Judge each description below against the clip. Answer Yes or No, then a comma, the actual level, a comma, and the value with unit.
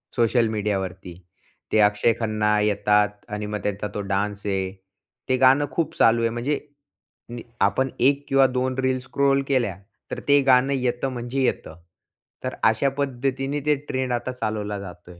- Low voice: Yes, low, 120 Hz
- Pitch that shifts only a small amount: No, average, 4.2 semitones